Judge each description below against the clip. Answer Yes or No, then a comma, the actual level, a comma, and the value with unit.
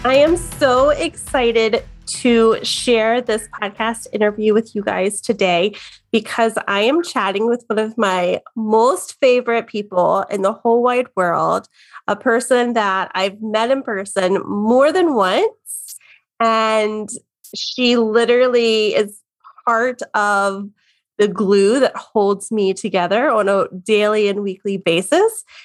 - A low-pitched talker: No, high, 220 Hz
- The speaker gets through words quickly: No, slow, 135 wpm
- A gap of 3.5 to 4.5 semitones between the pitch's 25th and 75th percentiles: No, average, 2.9 semitones